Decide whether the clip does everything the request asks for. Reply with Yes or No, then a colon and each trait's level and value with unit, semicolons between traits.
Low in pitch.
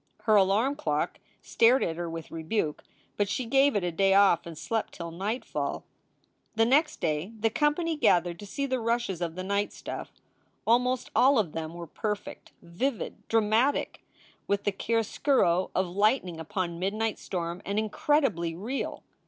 No: high, 205 Hz